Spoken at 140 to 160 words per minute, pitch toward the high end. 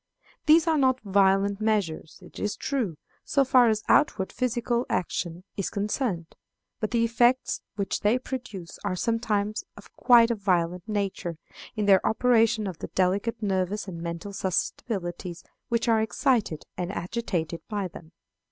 Yes: average, 150 wpm; high, 205 Hz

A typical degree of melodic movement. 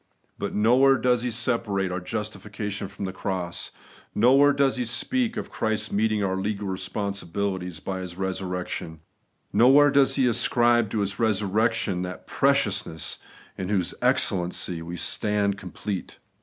Yes: average, 4.0 semitones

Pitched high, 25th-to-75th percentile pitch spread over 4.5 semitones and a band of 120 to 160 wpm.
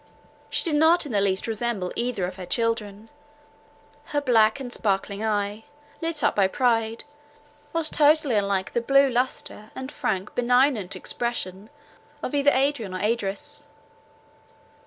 Yes: high, 230 Hz; average, 4.9 semitones; average, 140 wpm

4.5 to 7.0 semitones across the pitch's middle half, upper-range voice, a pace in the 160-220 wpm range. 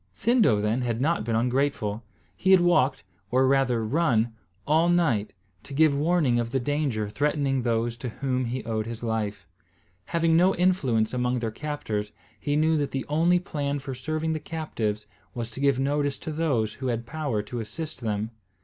No: average, 5.2 semitones; low, 130 Hz; average, 180 wpm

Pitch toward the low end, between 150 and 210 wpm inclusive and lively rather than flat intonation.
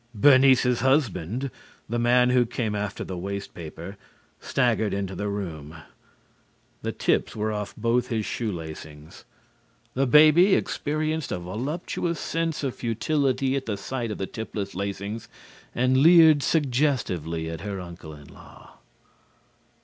No: low, 115 Hz; slow, 135 wpm; wide, 5.7 semitones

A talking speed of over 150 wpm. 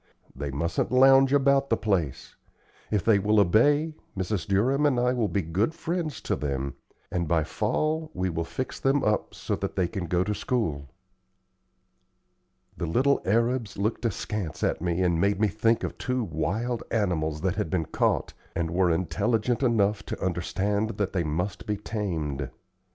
Yes: average, 170 wpm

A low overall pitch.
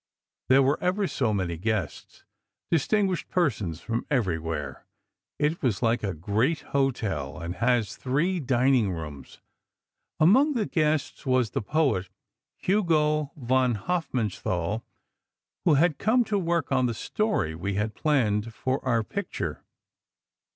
Yes: low, 130 Hz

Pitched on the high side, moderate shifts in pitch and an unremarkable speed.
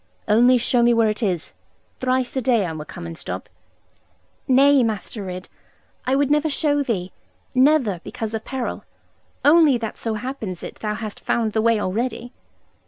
Yes: high, 230 Hz; average, 3.8 semitones; average, 175 wpm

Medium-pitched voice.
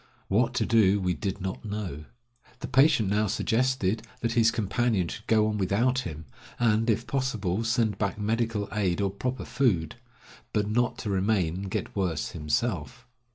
No: low, 105 Hz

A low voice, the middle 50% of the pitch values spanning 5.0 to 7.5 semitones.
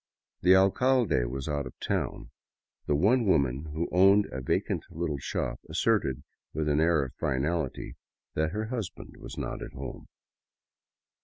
Yes: very low, 80 Hz; wide, 5.4 semitones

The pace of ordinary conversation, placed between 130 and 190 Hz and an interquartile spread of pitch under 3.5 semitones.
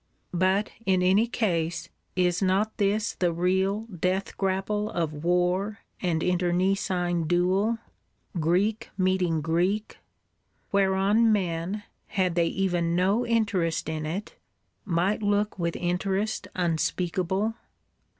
No: slow, 110 wpm; medium, 185 Hz; narrow, 2.6 semitones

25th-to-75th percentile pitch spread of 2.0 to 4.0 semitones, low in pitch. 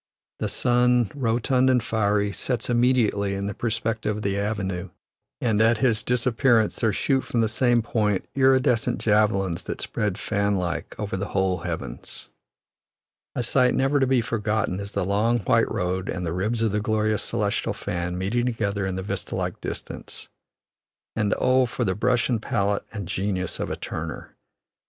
Yes: average, 3.3 semitones; low, 110 Hz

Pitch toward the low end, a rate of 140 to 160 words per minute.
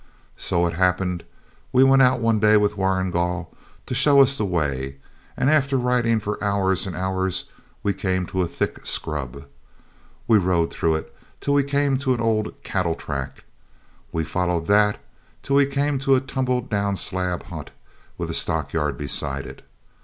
No: low, 100 Hz; average, 170 wpm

